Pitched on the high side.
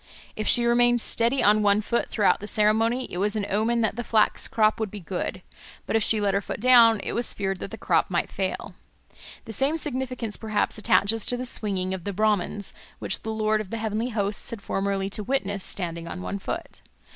Yes: high, 215 Hz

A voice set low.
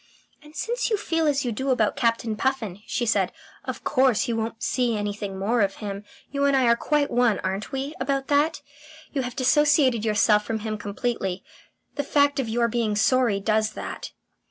No: high, 235 Hz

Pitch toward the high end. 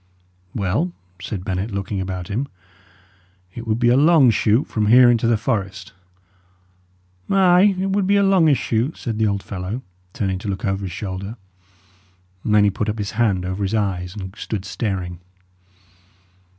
No: low, 105 Hz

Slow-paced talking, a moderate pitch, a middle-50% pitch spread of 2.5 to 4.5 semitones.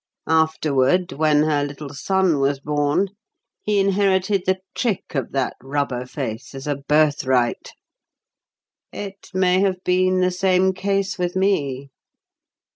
No: slow, 125 wpm; medium, 160 Hz; average, 5.0 semitones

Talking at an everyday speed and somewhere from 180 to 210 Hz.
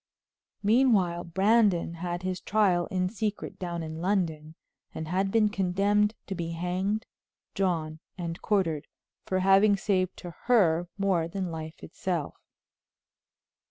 No: slow, 125 wpm; medium, 185 Hz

